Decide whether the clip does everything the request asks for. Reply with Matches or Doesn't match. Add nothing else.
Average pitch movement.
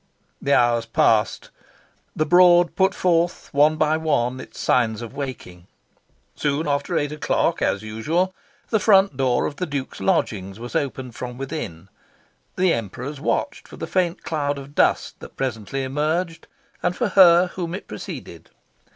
Doesn't match